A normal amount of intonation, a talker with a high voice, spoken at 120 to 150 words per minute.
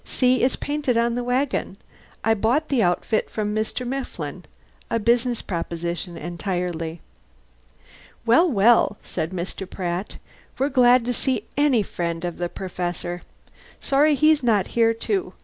No: wide, 6.2 semitones; high, 225 Hz; average, 140 wpm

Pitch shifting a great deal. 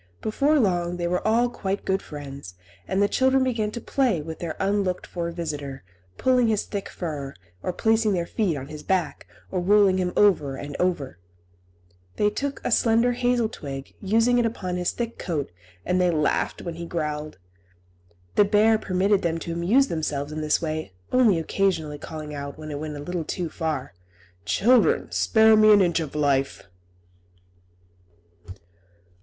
Yes: wide, 5.8 semitones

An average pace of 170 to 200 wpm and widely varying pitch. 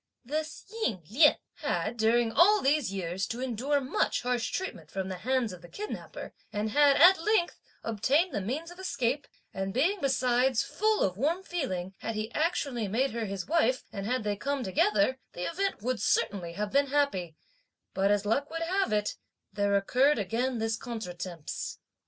Yes: average, 175 wpm; wide, 6.3 semitones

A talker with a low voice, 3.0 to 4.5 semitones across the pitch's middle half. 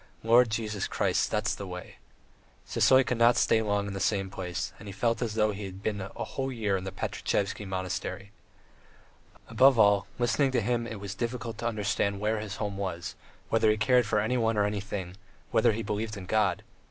No: low, 105 Hz; narrow, 2.6 semitones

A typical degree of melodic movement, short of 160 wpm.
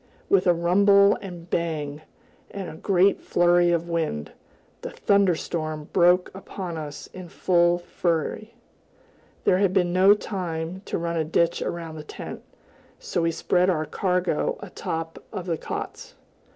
No: narrow, 2.3 semitones; average, 150 wpm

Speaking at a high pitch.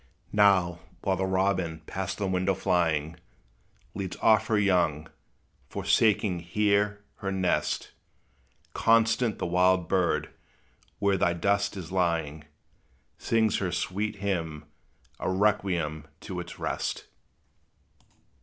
No: very low, 95 Hz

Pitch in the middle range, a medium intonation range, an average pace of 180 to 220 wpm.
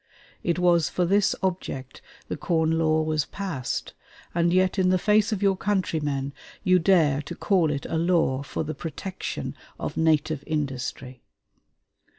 No: medium, 165 Hz; average, 3.9 semitones; average, 155 wpm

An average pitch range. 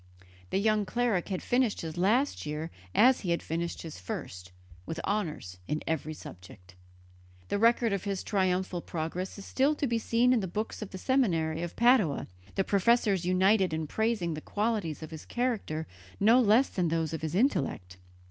No: wide, 5.9 semitones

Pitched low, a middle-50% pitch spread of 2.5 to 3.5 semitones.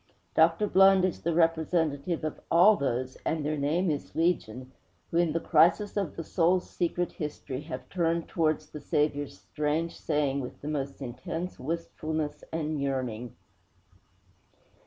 No: medium, 155 Hz; average, 3.1 semitones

